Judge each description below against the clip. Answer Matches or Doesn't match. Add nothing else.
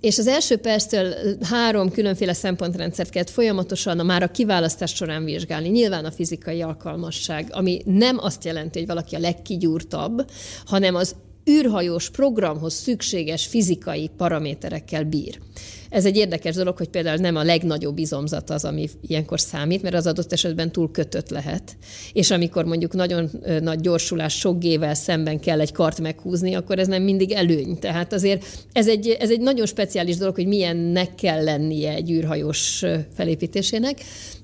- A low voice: Doesn't match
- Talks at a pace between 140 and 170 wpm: Matches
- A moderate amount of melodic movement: Matches